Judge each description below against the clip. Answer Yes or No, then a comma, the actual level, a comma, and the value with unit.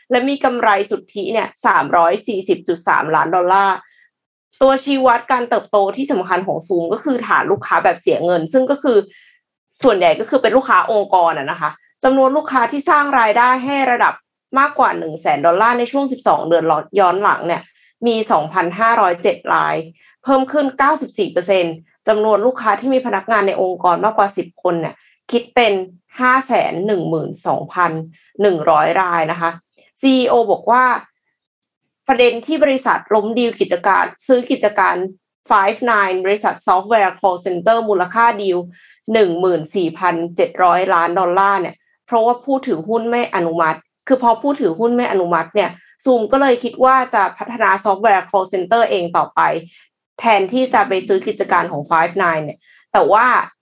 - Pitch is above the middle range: Yes, high, 215 Hz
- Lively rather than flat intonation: Yes, wide, 6.0 semitones